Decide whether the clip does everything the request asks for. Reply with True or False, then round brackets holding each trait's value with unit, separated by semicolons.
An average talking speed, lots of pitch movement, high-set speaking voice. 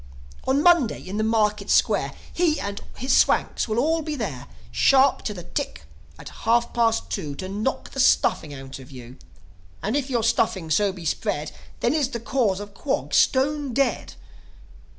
True (175 wpm; 6.1 semitones; 225 Hz)